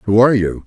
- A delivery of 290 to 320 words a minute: No, fast, 270 wpm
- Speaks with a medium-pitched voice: No, low, 110 Hz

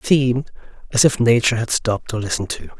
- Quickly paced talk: Yes, fast, 215 wpm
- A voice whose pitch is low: Yes, low, 120 Hz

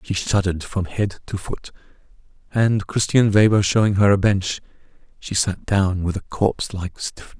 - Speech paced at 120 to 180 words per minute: Yes, average, 170 wpm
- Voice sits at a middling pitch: No, low, 100 Hz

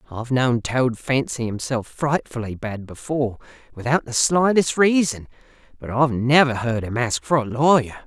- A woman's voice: No, male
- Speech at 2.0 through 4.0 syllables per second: No, 4.9 syllables/s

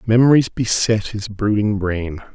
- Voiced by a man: Yes, male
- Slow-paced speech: Yes, slow, 130 wpm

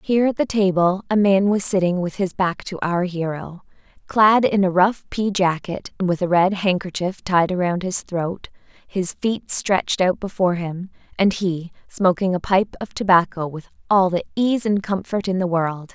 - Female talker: Yes, female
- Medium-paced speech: Yes, average, 190 wpm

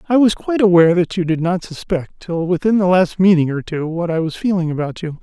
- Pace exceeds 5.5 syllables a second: Yes, 6.0 syllables/s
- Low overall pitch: No, medium, 175 Hz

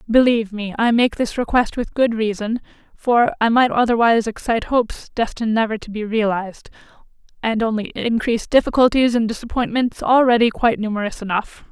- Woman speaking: Yes, female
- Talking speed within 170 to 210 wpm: No, average, 155 wpm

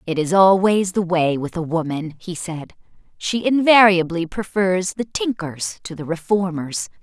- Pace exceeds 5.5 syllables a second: No, 4.3 syllables/s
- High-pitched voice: No, medium, 180 Hz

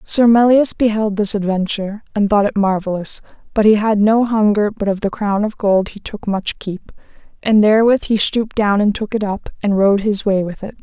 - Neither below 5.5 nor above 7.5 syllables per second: No, 5.2 syllables/s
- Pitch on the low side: No, high, 210 Hz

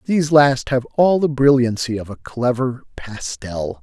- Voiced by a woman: No, male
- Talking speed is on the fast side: No, average, 155 wpm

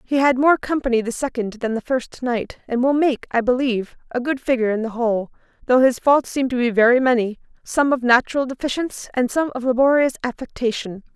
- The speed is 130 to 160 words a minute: No, fast, 205 wpm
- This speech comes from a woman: Yes, female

